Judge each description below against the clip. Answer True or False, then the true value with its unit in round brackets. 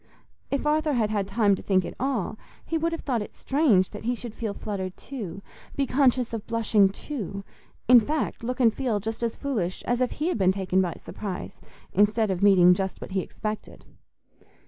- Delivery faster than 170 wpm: True (190 wpm)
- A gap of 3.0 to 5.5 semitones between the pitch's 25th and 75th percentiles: True (4.5 semitones)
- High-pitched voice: True (220 Hz)